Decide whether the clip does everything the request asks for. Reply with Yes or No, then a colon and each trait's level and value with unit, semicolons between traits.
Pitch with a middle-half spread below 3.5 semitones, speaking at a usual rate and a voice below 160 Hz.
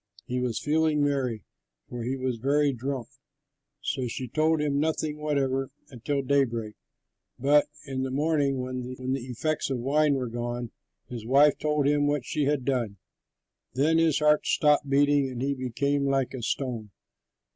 Yes: narrow, 2.6 semitones; average, 165 wpm; low, 135 Hz